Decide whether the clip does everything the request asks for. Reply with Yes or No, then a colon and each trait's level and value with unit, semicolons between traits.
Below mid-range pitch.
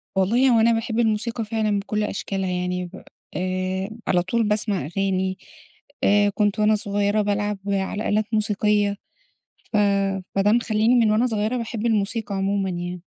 No: high, 205 Hz